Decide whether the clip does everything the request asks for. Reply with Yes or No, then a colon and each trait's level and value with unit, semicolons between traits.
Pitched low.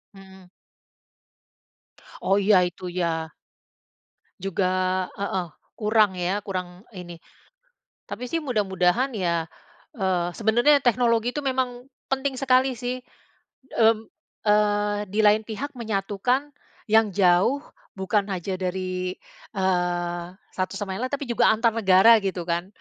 No: high, 205 Hz